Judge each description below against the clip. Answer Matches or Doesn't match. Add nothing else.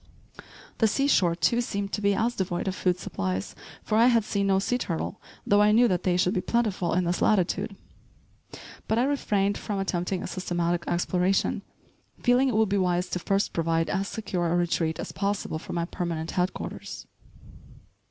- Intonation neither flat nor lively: Matches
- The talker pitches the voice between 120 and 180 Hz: Doesn't match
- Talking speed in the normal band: Matches